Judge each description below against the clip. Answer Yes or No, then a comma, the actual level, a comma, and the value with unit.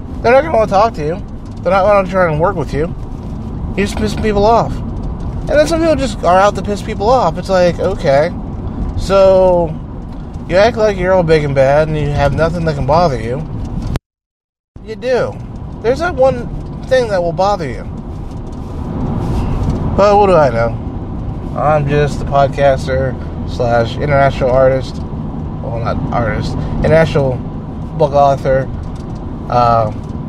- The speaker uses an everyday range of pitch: No, wide, 7.1 semitones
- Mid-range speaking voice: Yes, medium, 145 Hz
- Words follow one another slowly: No, average, 165 wpm